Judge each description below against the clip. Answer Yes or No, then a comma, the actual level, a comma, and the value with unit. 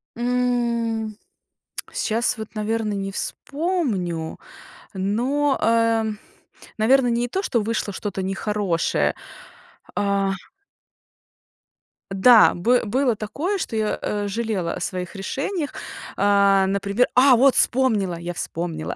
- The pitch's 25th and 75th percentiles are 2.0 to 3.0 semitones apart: No, average, 4.0 semitones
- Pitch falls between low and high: No, high, 220 Hz